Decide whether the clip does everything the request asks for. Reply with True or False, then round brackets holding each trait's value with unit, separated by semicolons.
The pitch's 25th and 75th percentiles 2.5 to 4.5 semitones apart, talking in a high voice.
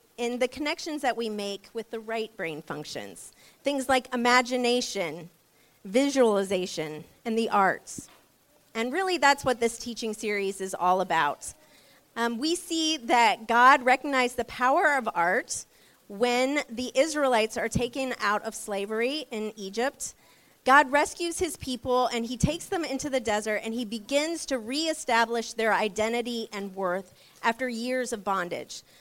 True (3.9 semitones; 235 Hz)